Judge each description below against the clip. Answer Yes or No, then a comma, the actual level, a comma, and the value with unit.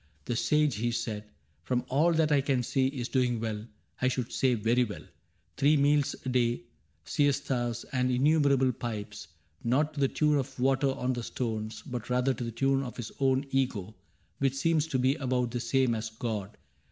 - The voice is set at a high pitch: No, low, 125 Hz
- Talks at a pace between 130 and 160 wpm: No, average, 200 wpm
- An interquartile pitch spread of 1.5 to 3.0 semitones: Yes, average, 2.7 semitones